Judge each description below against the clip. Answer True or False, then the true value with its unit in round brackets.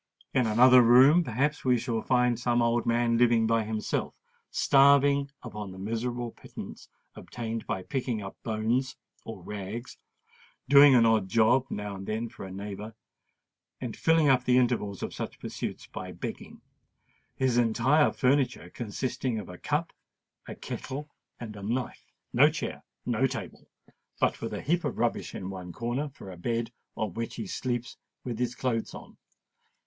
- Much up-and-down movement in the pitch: False (2.9 semitones)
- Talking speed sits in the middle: True (155 wpm)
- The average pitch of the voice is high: False (120 Hz)